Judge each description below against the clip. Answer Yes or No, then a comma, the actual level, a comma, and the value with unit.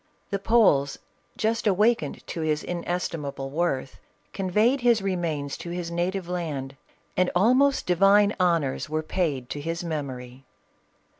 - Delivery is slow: Yes, slow, 130 wpm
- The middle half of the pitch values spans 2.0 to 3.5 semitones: No, average, 5.1 semitones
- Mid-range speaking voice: Yes, medium, 175 Hz